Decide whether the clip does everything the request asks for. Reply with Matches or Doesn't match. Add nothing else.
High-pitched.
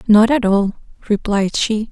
Matches